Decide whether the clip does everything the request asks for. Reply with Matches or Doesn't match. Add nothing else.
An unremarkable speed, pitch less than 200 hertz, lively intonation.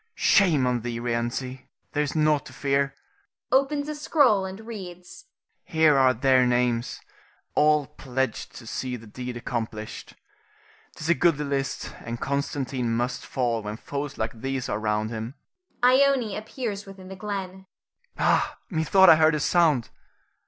Matches